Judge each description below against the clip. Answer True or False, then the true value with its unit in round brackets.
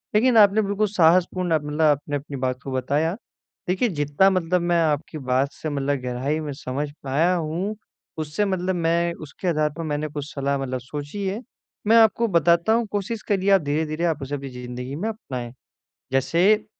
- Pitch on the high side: False (160 Hz)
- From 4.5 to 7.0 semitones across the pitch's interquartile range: True (5.0 semitones)